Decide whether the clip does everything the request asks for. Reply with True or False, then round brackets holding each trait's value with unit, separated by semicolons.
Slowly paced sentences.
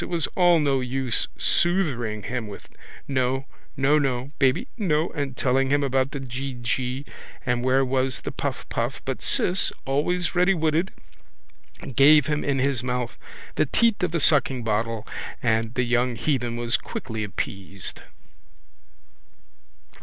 True (130 wpm)